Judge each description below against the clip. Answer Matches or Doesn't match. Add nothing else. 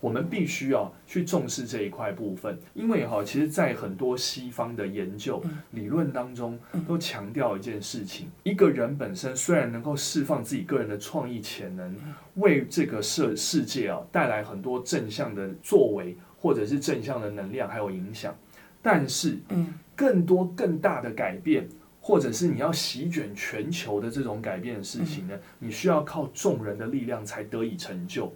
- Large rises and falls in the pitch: Matches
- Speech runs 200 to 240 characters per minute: Doesn't match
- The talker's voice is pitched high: Doesn't match